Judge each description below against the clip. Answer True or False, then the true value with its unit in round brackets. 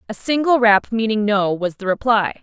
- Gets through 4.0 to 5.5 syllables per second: True (5.0 syllables/s)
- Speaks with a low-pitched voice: False (215 Hz)